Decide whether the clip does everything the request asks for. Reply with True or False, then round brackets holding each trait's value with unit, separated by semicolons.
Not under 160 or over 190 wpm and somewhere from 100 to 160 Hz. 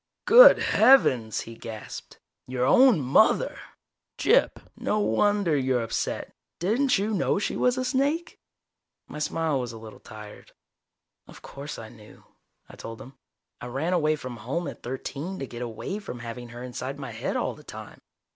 True (165 wpm; 140 Hz)